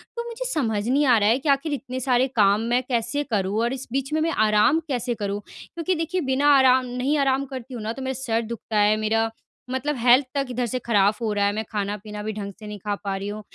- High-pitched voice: Yes, high, 240 Hz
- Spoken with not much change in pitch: No, average, 4.2 semitones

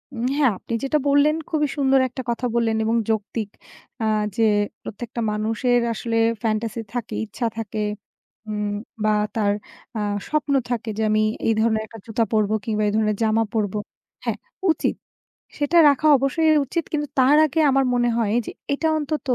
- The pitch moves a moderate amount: Yes, average, 4.0 semitones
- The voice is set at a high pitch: Yes, high, 230 Hz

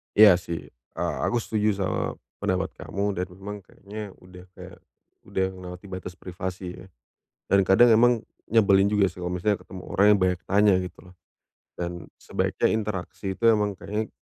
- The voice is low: Yes, very low, 95 Hz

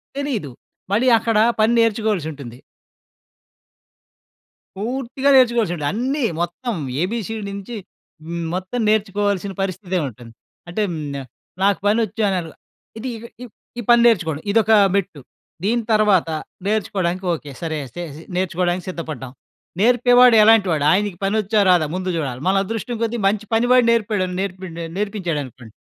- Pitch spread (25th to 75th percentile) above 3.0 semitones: Yes, average, 4.6 semitones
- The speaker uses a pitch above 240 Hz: No, high, 200 Hz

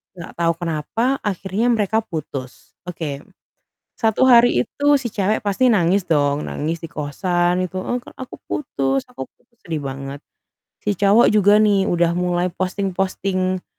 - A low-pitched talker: No, medium, 185 Hz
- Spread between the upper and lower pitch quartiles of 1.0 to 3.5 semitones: No, average, 4.3 semitones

